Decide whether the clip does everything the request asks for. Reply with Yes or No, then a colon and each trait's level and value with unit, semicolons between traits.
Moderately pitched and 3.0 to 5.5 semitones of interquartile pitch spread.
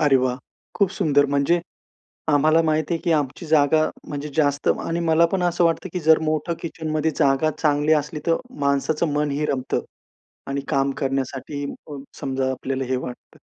No: medium, 150 Hz; narrow, 2.5 semitones